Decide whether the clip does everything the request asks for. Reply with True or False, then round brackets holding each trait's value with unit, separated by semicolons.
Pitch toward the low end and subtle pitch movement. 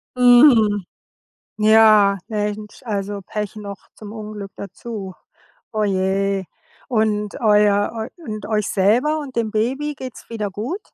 False (215 Hz; 2.1 semitones)